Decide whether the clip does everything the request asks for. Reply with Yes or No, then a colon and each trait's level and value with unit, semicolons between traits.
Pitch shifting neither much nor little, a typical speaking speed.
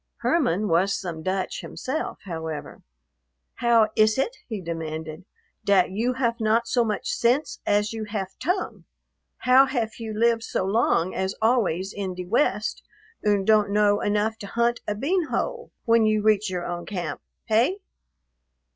Yes: average, 3.8 semitones; average, 155 wpm